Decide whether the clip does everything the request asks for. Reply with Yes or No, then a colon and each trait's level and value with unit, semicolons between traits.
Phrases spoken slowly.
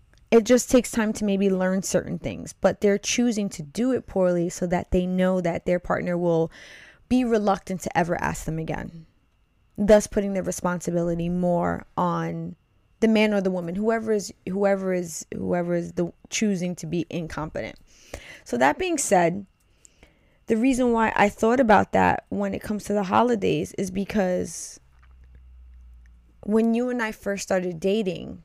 No: average, 165 wpm